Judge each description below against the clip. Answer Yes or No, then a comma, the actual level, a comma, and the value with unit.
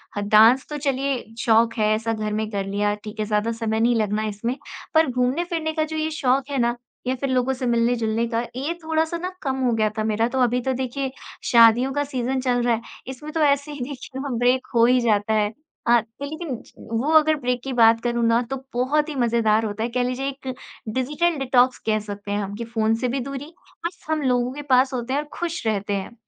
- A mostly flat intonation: No, average, 3.5 semitones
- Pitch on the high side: Yes, high, 245 Hz